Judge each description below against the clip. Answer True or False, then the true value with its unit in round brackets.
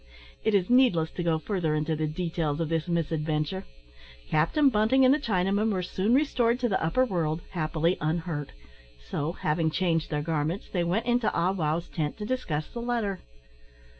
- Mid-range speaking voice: True (170 Hz)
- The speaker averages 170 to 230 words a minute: True (175 wpm)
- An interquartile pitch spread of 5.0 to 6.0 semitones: True (5.3 semitones)